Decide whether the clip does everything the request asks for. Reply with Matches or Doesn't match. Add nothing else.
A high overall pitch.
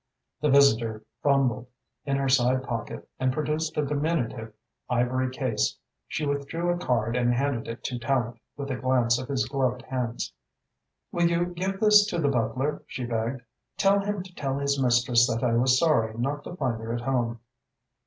Doesn't match